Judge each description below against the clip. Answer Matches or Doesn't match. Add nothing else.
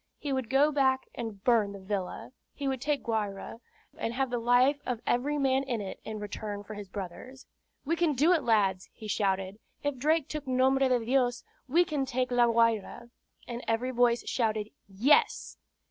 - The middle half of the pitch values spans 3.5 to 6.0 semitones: Matches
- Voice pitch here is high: Matches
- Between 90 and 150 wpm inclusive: Doesn't match